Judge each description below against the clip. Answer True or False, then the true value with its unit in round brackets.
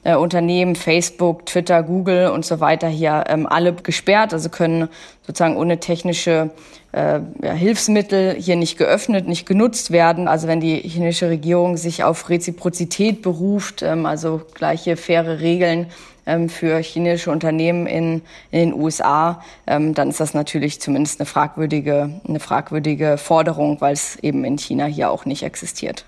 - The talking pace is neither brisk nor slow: True (155 wpm)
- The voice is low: False (170 Hz)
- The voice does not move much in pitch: True (1.7 semitones)